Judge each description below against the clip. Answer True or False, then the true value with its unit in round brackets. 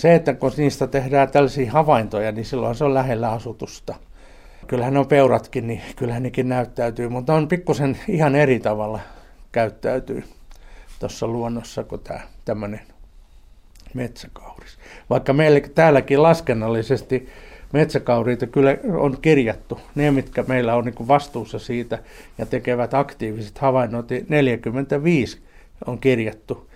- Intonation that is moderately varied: True (3.3 semitones)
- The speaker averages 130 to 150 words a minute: False (120 wpm)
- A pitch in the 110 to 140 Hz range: True (125 Hz)